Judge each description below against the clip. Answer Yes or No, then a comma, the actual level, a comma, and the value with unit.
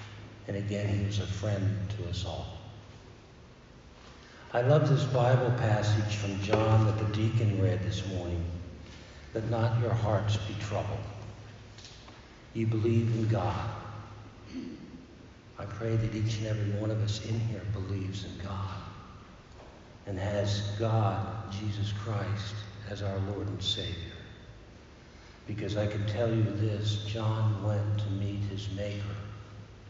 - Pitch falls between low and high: No, low, 105 Hz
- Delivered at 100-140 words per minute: Yes, slow, 135 wpm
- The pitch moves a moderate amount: No, narrow, 1.7 semitones